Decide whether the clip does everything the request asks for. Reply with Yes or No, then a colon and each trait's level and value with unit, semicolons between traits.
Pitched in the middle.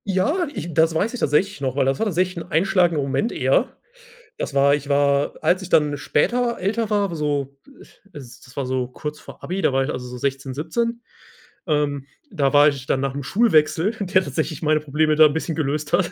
Yes: medium, 150 Hz